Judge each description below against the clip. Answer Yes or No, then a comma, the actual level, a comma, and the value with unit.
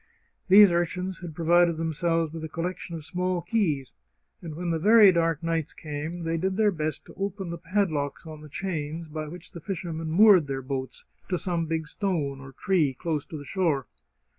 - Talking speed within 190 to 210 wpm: Yes, average, 195 wpm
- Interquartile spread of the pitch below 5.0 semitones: Yes, average, 2.8 semitones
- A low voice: No, medium, 165 Hz